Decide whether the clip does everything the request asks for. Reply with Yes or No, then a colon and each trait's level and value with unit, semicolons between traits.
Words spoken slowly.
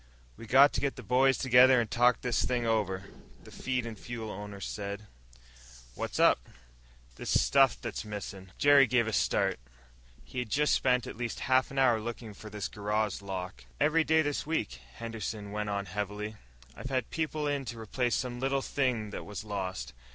No: average, 190 wpm